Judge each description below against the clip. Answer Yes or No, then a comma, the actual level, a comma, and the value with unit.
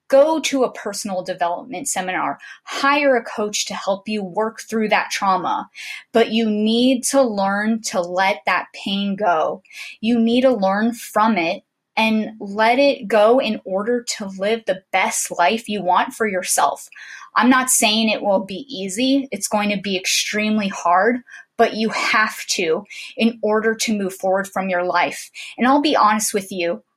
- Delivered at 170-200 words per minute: Yes, average, 175 wpm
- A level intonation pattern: No, average, 3.3 semitones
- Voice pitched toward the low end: No, high, 215 Hz